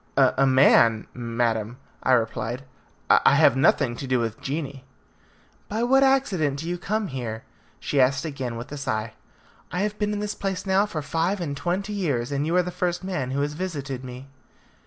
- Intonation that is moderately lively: No, wide, 6.6 semitones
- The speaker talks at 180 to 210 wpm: Yes, average, 190 wpm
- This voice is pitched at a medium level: Yes, medium, 145 Hz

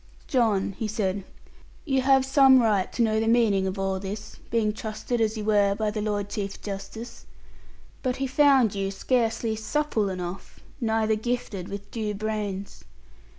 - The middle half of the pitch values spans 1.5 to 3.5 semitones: Yes, average, 2.9 semitones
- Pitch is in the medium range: No, high, 215 Hz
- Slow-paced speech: No, average, 160 wpm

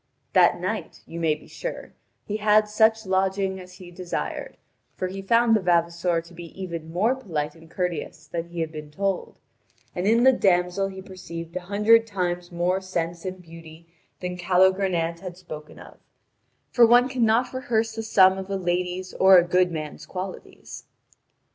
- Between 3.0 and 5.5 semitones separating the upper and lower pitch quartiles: No, narrow, 2.6 semitones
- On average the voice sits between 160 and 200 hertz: Yes, medium, 185 Hz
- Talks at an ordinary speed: Yes, average, 175 wpm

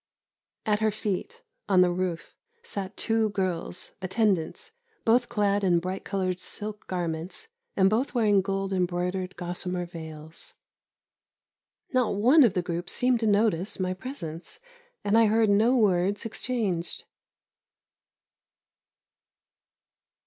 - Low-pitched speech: No, high, 195 Hz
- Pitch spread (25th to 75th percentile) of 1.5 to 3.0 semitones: No, average, 3.4 semitones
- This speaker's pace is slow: Yes, slow, 120 wpm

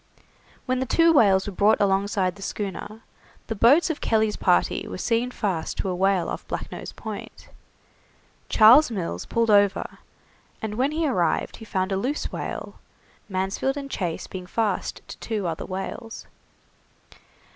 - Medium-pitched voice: No, high, 210 Hz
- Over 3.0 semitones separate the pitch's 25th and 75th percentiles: Yes, average, 4.0 semitones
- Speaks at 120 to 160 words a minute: Yes, average, 155 wpm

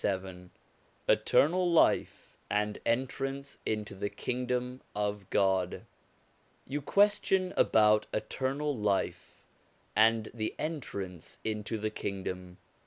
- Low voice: Yes, low, 110 Hz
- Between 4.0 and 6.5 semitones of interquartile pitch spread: Yes, average, 5.2 semitones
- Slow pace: Yes, slow, 100 wpm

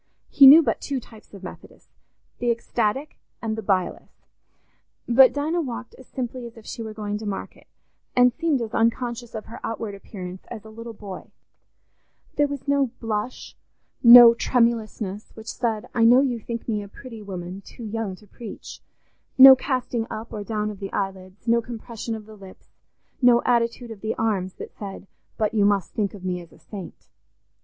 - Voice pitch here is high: Yes, high, 225 Hz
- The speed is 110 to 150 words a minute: No, average, 180 wpm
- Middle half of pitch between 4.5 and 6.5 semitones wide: No, average, 2.8 semitones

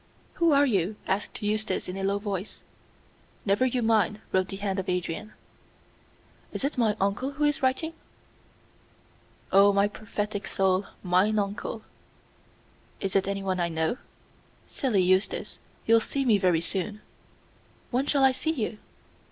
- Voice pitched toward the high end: Yes, high, 205 Hz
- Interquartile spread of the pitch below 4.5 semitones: Yes, average, 3.7 semitones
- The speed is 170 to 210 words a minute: No, average, 145 wpm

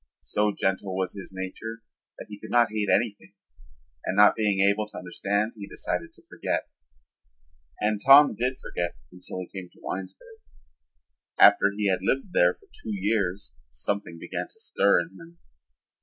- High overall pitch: No, low, 100 Hz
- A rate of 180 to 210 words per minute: No, average, 165 wpm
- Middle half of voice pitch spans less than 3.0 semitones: Yes, narrow, 2.6 semitones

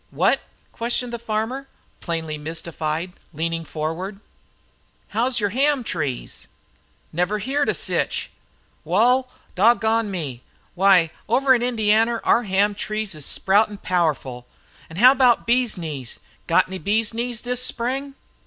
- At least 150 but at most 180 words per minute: No, slow, 135 wpm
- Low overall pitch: No, high, 210 Hz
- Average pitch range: No, wide, 6.2 semitones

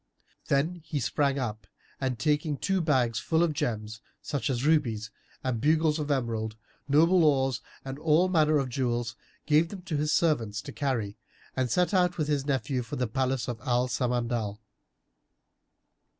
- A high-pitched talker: No, low, 135 Hz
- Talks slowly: No, average, 160 wpm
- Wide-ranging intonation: No, average, 4.3 semitones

